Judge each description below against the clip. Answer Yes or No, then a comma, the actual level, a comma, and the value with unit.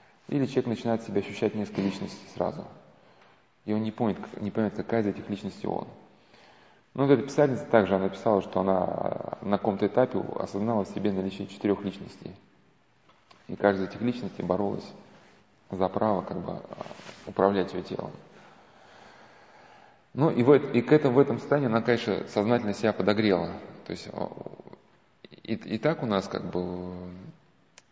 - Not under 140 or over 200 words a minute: Yes, average, 155 wpm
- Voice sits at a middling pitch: No, low, 105 Hz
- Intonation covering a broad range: No, average, 3.7 semitones